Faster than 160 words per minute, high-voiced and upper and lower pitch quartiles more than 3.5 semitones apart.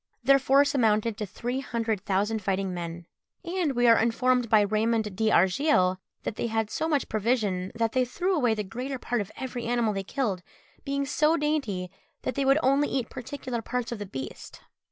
Yes: average, 190 wpm; high, 230 Hz; average, 4.4 semitones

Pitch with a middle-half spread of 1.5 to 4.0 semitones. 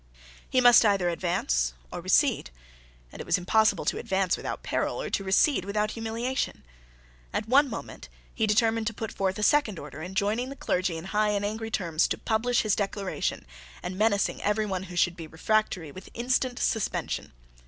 Yes: average, 3.4 semitones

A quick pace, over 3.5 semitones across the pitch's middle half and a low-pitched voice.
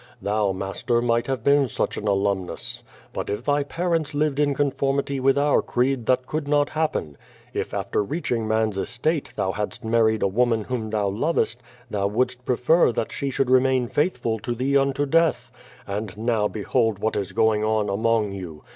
No: average, 180 wpm; average, 4.7 semitones; low, 120 Hz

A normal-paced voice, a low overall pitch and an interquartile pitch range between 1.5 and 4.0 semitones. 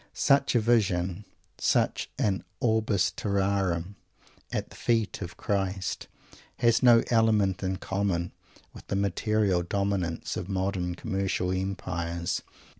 No: slow, 115 wpm; low, 100 Hz; average, 2.7 semitones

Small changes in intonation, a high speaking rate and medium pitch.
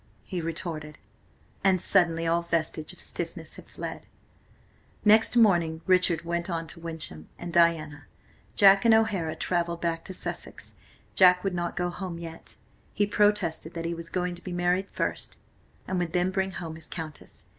No: narrow, 2.1 semitones; average, 165 wpm; medium, 170 Hz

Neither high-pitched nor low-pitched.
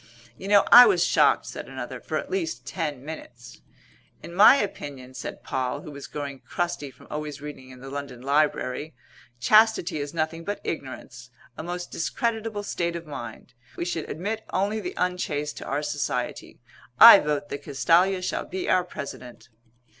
Yes: medium, 155 Hz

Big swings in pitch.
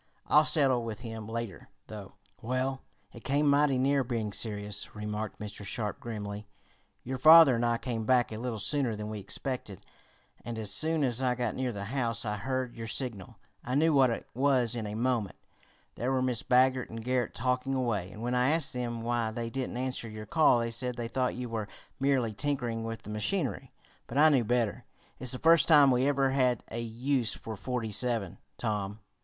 No: average, 2.9 semitones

